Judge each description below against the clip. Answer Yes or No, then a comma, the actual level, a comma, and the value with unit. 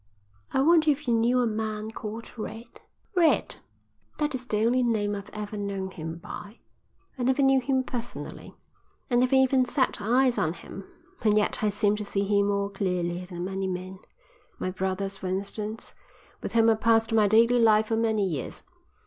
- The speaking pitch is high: Yes, high, 215 Hz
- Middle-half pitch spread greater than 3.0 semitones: Yes, average, 3.6 semitones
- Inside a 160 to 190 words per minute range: Yes, average, 185 wpm